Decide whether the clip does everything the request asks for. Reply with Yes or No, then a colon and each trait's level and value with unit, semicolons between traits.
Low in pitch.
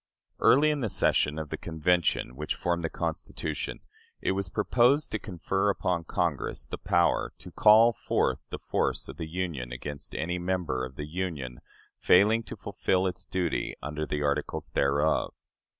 Yes: very low, 85 Hz